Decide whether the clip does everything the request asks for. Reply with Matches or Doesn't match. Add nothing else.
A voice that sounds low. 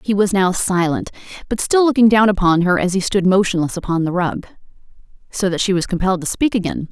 Doesn't match